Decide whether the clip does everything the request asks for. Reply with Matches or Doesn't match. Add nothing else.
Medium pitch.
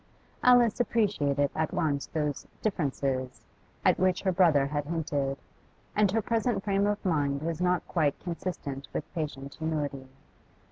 Matches